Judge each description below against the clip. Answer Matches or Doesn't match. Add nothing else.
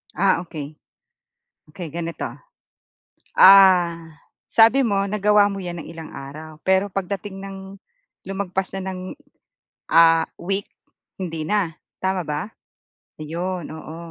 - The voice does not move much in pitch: Doesn't match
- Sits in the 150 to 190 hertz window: Matches